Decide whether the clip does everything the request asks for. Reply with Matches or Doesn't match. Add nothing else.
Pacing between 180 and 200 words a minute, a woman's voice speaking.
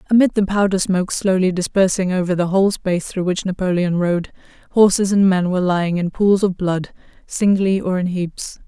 Matches